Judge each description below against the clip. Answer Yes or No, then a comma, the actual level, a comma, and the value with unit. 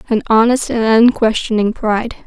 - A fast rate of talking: No, slow, 130 wpm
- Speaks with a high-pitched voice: Yes, high, 225 Hz